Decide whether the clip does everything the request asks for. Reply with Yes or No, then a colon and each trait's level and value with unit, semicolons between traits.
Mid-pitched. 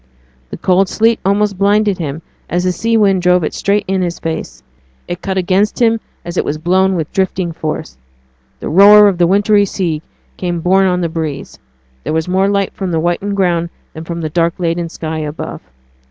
Yes: medium, 180 Hz